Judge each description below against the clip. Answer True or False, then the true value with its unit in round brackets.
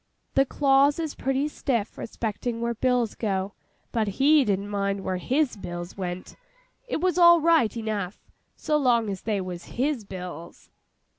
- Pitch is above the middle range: True (230 Hz)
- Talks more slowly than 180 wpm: True (155 wpm)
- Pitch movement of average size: False (5.8 semitones)